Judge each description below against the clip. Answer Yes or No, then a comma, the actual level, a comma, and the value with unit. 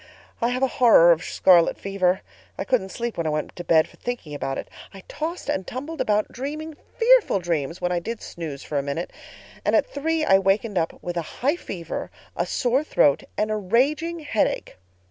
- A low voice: No, high, 205 Hz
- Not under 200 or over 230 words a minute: Yes, fast, 205 wpm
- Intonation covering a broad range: Yes, wide, 7.8 semitones